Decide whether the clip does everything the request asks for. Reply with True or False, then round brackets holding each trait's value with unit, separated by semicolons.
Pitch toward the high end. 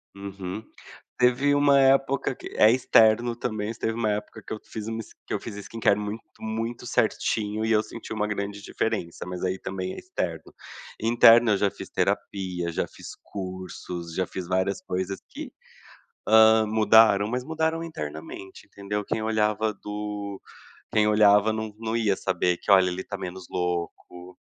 False (105 Hz)